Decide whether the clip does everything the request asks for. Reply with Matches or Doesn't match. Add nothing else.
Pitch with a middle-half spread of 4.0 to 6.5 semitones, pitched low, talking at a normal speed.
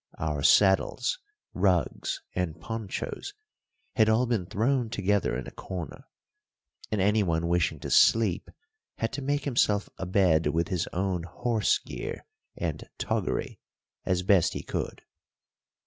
Doesn't match